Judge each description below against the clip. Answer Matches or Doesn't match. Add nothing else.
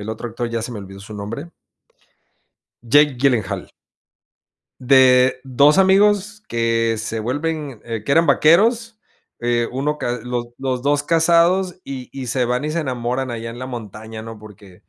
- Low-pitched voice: Matches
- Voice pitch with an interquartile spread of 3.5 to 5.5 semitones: Matches